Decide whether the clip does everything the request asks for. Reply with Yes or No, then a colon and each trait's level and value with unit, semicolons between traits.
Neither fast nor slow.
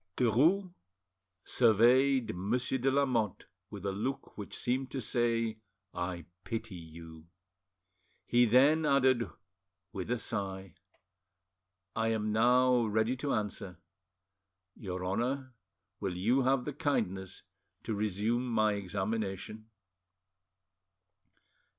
No: slow, 105 wpm